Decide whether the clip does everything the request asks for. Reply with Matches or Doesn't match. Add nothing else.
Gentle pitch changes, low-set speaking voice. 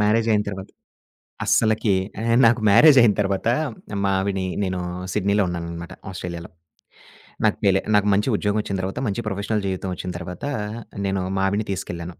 Matches